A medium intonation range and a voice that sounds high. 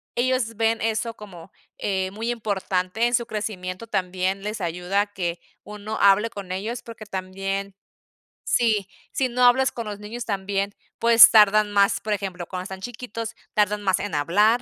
Yes: average, 3.0 semitones; high, 205 Hz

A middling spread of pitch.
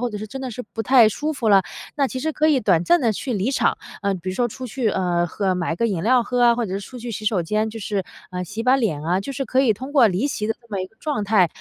Yes: average, 4.8 semitones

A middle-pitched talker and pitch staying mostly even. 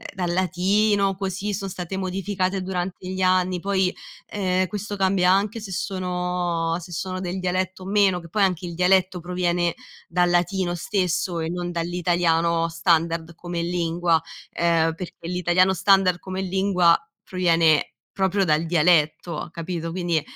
Yes: medium, 180 Hz; narrow, 1.8 semitones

